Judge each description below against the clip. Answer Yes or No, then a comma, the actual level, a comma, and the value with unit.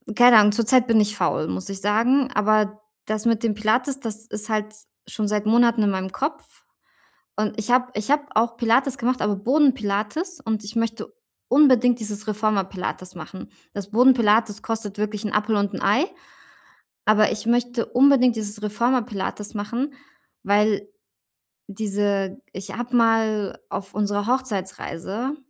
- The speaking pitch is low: No, high, 215 Hz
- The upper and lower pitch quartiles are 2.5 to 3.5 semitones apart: Yes, average, 2.8 semitones